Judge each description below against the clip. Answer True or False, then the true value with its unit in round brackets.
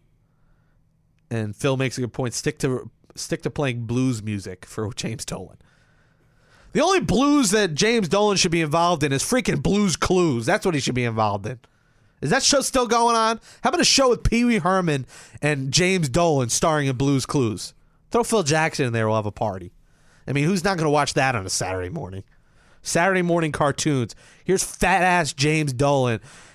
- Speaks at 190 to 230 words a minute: True (200 wpm)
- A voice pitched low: False (150 Hz)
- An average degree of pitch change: False (6.7 semitones)